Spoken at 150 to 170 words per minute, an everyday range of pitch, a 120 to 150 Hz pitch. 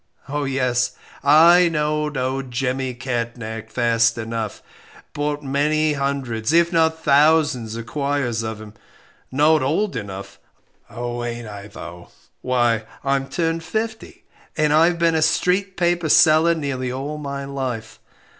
No: slow, 135 wpm; average, 4.6 semitones; medium, 140 Hz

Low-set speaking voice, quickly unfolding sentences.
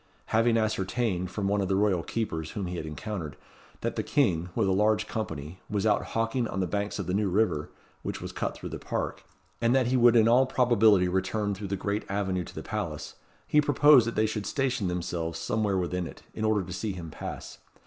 Yes: low, 100 Hz; fast, 220 wpm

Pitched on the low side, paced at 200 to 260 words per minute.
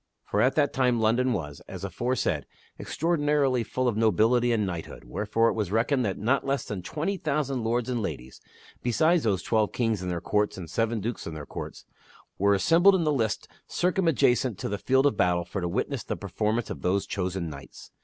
Yes: low, 115 Hz; fast, 205 wpm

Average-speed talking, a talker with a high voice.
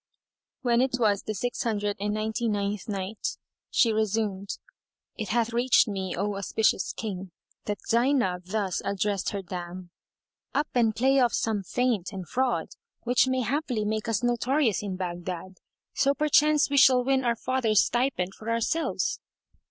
Yes: average, 155 wpm; high, 220 Hz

